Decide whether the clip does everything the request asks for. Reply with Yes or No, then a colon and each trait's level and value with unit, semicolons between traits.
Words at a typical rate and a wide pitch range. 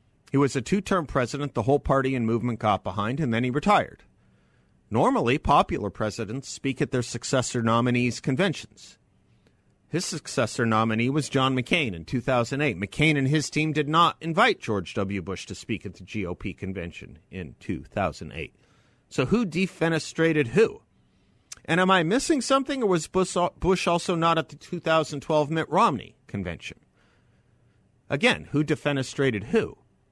Yes: average, 150 wpm; wide, 6.3 semitones